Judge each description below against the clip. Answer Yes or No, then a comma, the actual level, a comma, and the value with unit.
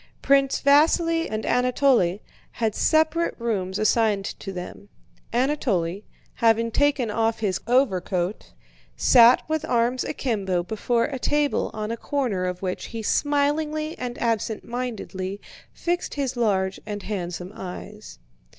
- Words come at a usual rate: No, slow, 125 wpm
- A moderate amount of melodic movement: No, wide, 6.0 semitones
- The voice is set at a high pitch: Yes, high, 230 Hz